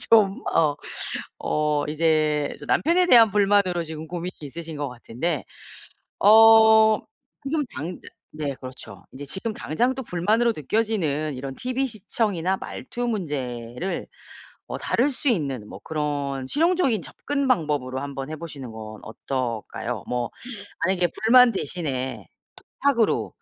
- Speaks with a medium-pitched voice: Yes, medium, 165 Hz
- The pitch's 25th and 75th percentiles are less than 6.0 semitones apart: No, wide, 7.9 semitones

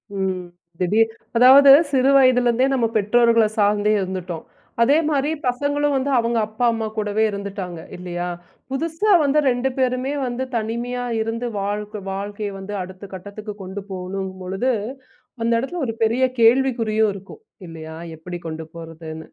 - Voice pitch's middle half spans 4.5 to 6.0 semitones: Yes, average, 4.8 semitones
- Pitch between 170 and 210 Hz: No, high, 220 Hz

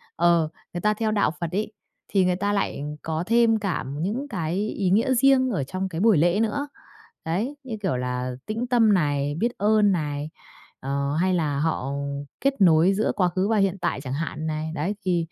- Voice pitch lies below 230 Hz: Yes, medium, 185 Hz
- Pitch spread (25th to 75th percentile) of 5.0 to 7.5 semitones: Yes, wide, 5.4 semitones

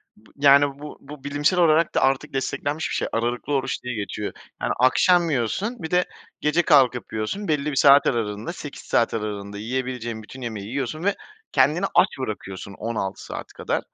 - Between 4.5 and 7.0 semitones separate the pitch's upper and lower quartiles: Yes, average, 4.8 semitones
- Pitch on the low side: Yes, low, 130 Hz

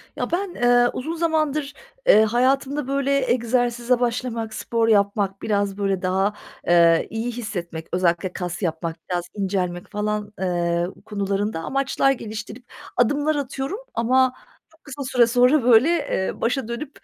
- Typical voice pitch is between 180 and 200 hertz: No, high, 230 Hz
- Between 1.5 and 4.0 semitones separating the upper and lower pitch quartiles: No, average, 5.2 semitones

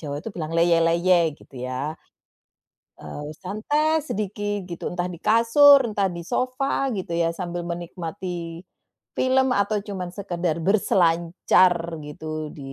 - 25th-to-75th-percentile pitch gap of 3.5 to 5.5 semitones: Yes, average, 4.2 semitones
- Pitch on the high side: No, medium, 180 Hz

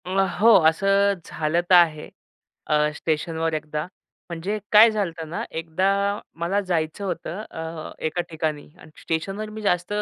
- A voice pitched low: No, medium, 170 Hz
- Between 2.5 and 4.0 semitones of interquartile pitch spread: Yes, average, 3.6 semitones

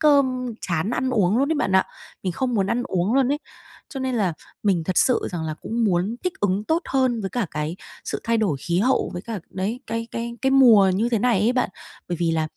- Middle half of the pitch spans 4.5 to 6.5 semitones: Yes, average, 5.3 semitones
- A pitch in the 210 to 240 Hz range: Yes, high, 225 Hz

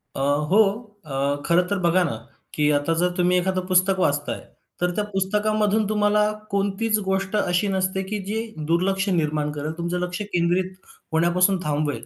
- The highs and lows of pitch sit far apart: No, average, 2.9 semitones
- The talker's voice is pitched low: No, medium, 185 Hz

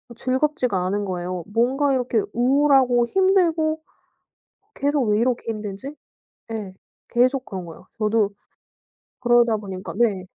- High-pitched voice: Yes, high, 240 Hz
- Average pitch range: Yes, average, 4.9 semitones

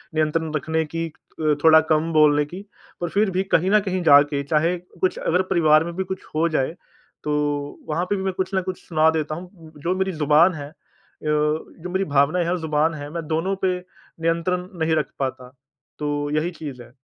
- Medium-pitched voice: Yes, medium, 160 Hz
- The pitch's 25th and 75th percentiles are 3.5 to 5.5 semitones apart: No, average, 2.9 semitones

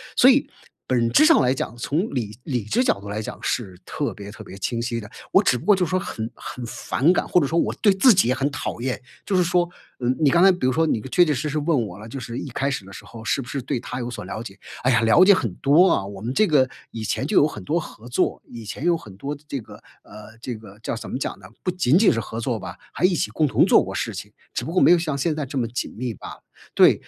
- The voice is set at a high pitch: No, low, 130 Hz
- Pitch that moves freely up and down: Yes, wide, 6.4 semitones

